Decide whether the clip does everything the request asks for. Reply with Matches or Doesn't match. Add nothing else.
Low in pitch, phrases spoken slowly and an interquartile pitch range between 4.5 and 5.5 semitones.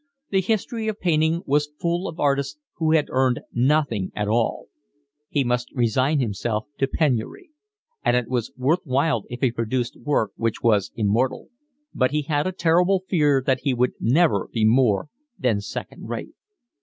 Doesn't match